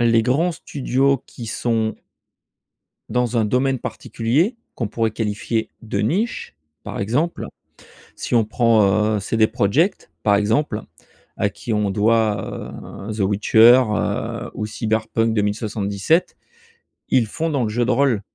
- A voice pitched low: Yes, low, 115 Hz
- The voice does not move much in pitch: No, average, 3.1 semitones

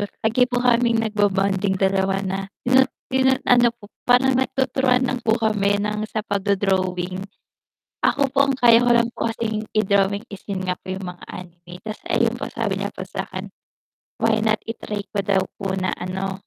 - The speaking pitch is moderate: No, high, 205 Hz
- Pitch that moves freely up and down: No, average, 3.7 semitones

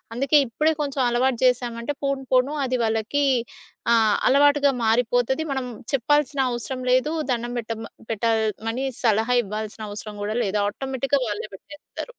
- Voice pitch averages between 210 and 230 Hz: No, high, 245 Hz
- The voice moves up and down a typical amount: Yes, average, 3.6 semitones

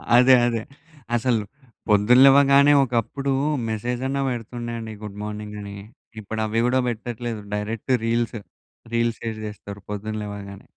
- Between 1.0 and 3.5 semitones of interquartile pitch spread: Yes, narrow, 2.6 semitones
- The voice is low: Yes, low, 115 Hz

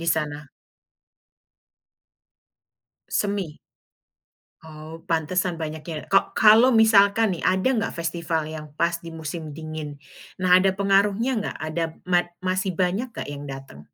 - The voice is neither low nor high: Yes, medium, 170 Hz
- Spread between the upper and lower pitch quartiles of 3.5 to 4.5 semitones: Yes, average, 3.8 semitones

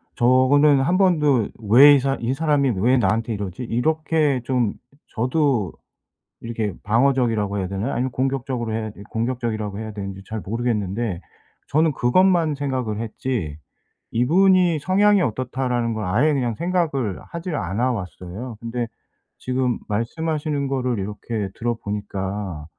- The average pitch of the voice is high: No, low, 120 Hz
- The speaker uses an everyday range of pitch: Yes, average, 4.7 semitones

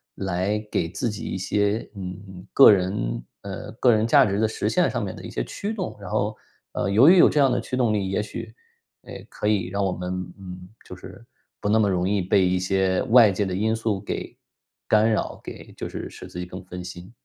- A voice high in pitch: No, low, 100 Hz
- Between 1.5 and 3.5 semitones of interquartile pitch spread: Yes, average, 3.2 semitones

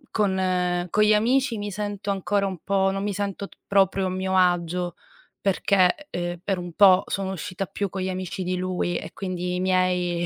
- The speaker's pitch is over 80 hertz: Yes, high, 190 Hz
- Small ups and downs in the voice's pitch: Yes, narrow, 1.7 semitones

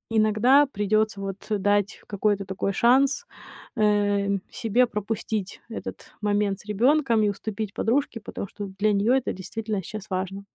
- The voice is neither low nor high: No, high, 210 Hz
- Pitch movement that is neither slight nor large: No, narrow, 2.0 semitones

